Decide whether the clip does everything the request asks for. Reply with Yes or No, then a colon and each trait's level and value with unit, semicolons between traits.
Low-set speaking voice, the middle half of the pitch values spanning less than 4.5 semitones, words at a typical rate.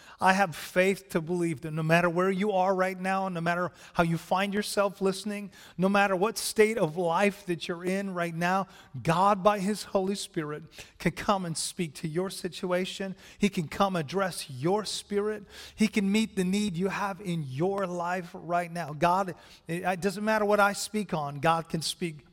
No: medium, 185 Hz; narrow, 2.6 semitones; average, 195 wpm